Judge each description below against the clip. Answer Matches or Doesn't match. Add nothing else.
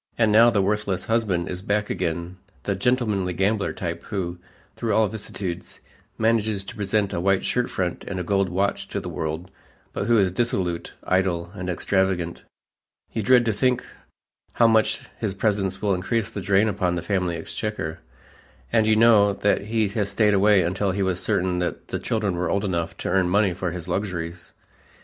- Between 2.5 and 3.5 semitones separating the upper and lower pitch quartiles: Matches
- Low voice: Matches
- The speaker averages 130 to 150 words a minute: Doesn't match